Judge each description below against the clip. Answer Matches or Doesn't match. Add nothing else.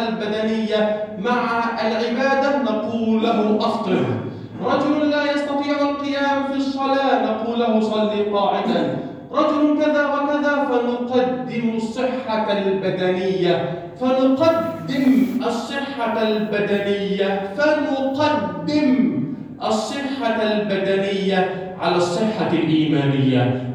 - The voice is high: Matches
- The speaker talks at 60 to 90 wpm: Matches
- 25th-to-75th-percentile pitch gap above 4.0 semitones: Matches